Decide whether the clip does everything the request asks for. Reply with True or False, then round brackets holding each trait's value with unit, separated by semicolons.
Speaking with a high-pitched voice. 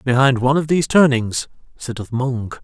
False (130 Hz)